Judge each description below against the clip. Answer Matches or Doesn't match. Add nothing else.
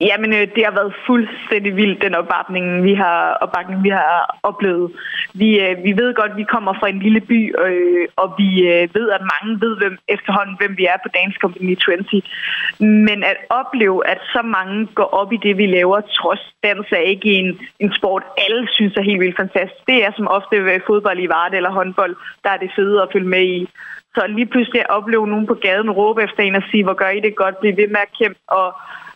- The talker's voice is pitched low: Doesn't match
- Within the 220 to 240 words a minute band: Matches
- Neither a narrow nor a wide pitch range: Doesn't match